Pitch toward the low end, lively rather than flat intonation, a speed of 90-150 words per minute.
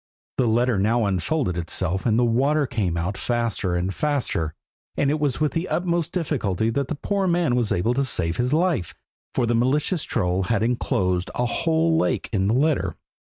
No: low, 120 Hz; wide, 7.6 semitones; average, 185 wpm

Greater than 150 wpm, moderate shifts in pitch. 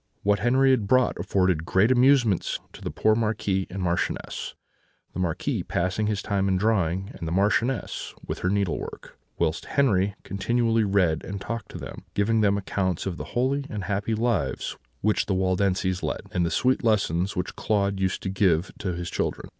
Yes: average, 180 wpm; average, 3.1 semitones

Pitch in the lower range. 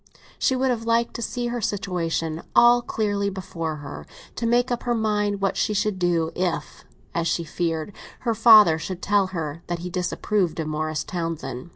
No: medium, 185 Hz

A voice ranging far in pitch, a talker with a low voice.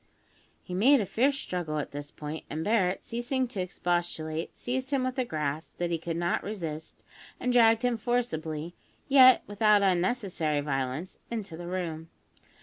No: wide, 6.9 semitones; medium, 180 Hz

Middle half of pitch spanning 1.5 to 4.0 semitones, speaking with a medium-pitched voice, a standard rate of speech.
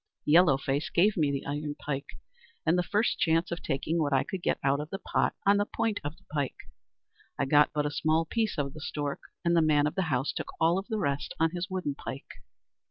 No: average, 3.6 semitones; medium, 155 Hz; fast, 230 wpm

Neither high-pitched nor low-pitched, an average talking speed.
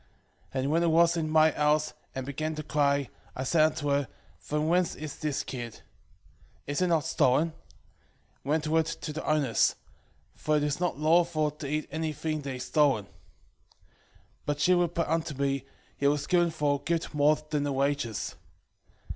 Yes: medium, 150 Hz; average, 180 wpm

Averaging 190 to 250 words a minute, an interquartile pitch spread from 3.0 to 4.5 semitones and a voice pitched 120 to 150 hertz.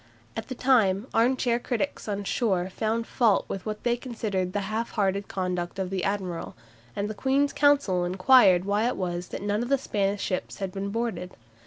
No: average, 195 wpm; average, 3.9 semitones; high, 205 Hz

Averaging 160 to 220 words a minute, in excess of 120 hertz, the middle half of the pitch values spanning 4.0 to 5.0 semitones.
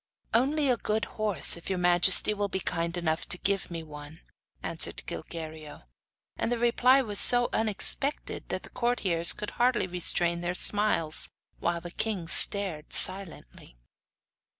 No: average, 150 wpm; medium, 185 Hz; average, 4.7 semitones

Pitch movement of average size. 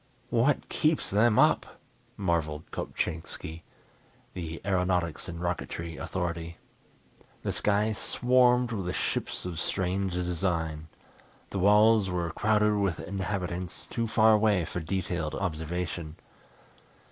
Yes: average, 3.8 semitones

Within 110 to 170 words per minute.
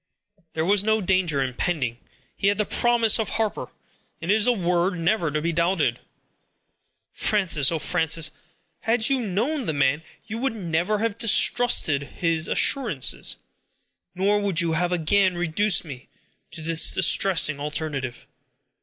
Yes: average, 145 wpm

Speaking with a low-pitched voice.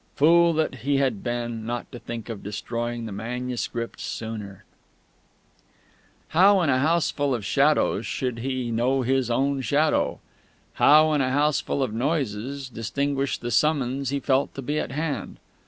Yes: low, 130 Hz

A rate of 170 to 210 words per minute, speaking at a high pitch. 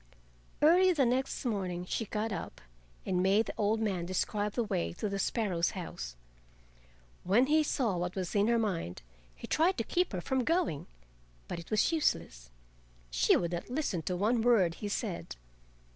Yes: average, 175 wpm; high, 205 Hz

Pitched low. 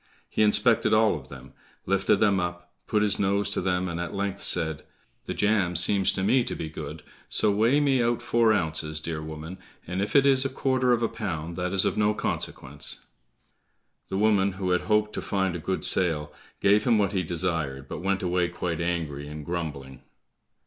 Yes: very low, 95 Hz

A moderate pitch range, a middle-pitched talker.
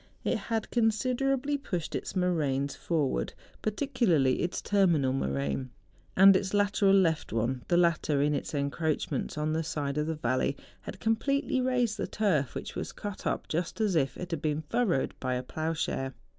No: wide, 6.7 semitones; medium, 165 Hz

